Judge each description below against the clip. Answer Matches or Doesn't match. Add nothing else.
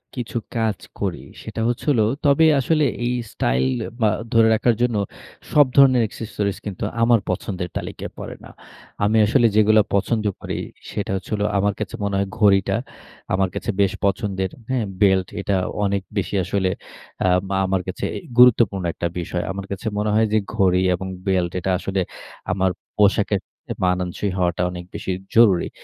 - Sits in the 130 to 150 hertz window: Doesn't match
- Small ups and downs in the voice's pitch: Doesn't match